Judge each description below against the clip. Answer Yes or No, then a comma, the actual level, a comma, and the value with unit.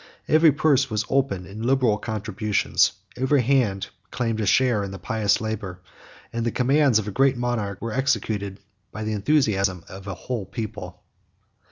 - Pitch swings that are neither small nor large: Yes, average, 4.4 semitones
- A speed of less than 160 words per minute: No, average, 165 wpm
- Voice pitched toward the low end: Yes, low, 110 Hz